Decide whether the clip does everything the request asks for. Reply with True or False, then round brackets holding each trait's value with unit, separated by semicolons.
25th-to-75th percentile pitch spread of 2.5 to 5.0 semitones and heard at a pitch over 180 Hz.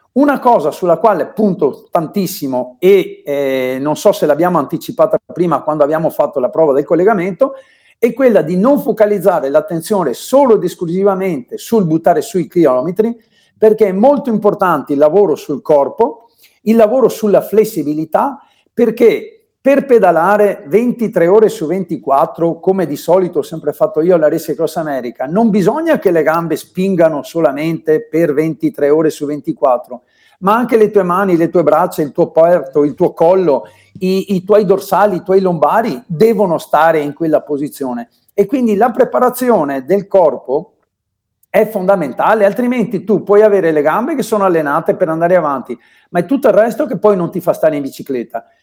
False (5.4 semitones; 190 Hz)